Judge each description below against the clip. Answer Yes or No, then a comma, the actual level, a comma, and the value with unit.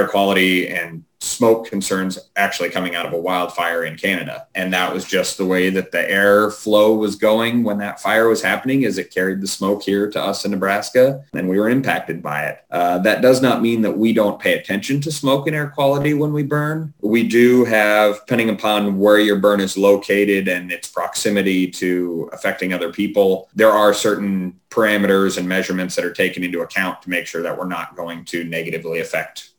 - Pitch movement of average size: Yes, average, 3.4 semitones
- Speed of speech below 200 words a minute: No, fast, 205 wpm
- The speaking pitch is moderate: No, low, 100 Hz